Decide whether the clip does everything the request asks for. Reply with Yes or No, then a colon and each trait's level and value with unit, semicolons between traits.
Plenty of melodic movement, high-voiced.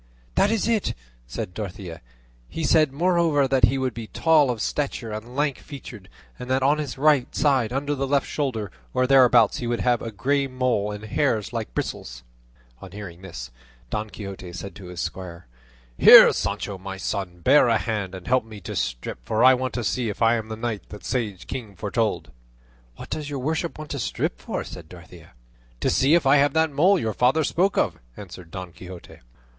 No: wide, 5.9 semitones; low, 120 Hz